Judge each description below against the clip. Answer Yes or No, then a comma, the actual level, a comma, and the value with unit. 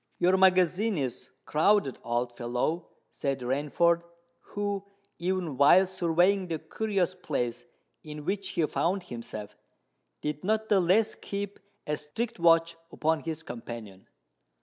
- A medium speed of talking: No, slow, 125 wpm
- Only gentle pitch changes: No, average, 4.9 semitones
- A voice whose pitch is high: No, medium, 170 Hz